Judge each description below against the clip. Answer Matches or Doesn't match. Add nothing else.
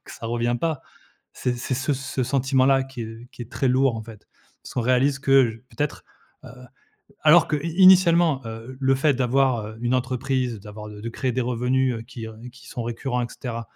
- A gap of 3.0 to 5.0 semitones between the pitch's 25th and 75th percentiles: Doesn't match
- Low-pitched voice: Matches